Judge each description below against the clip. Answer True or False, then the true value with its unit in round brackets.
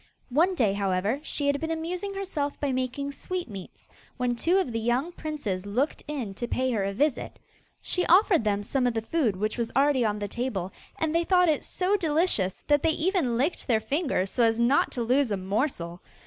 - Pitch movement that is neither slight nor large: False (6.7 semitones)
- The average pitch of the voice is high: True (260 Hz)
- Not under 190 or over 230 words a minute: True (205 wpm)